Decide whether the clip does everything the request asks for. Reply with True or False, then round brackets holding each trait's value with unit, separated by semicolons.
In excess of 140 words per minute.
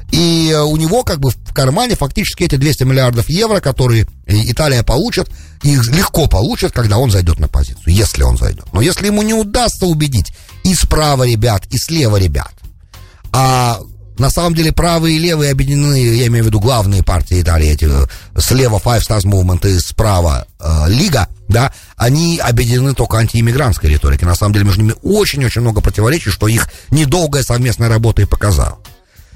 True (170 wpm)